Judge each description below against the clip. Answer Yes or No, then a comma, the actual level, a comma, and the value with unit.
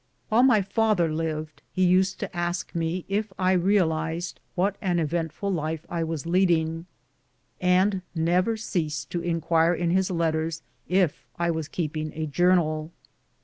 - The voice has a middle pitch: Yes, medium, 170 Hz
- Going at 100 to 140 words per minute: No, average, 155 wpm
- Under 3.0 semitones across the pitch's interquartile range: Yes, narrow, 2.5 semitones